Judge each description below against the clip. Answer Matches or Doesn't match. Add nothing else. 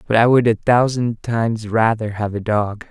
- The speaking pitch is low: Matches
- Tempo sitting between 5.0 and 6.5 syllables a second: Doesn't match